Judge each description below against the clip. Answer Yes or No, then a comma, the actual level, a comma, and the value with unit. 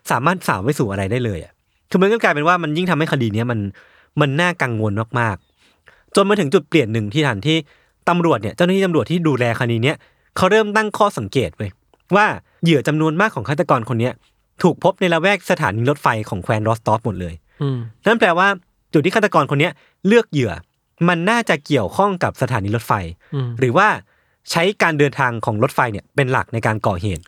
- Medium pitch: Yes, medium, 145 Hz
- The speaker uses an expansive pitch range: Yes, wide, 7.5 semitones